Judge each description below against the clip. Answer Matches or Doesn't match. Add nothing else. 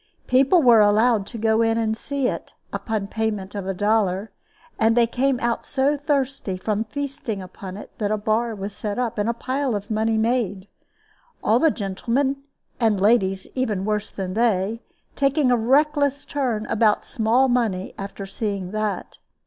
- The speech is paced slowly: Doesn't match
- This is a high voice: Matches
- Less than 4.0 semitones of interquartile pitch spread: Matches